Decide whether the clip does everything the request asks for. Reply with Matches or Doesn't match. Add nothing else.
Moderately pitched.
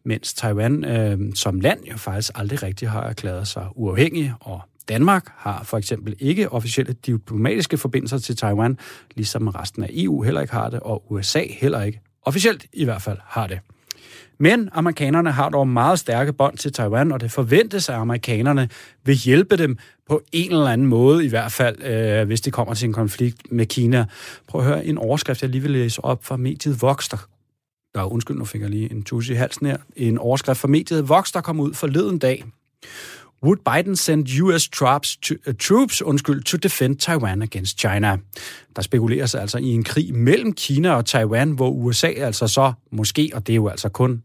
Doesn't match